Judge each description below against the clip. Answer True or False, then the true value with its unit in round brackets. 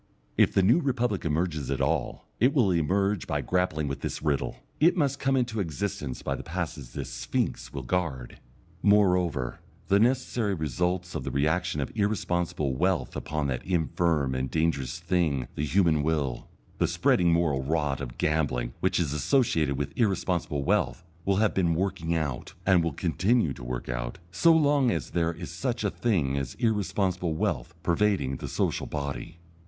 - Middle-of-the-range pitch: False (85 Hz)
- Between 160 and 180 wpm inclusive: True (170 wpm)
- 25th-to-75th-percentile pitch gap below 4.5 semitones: False (5.6 semitones)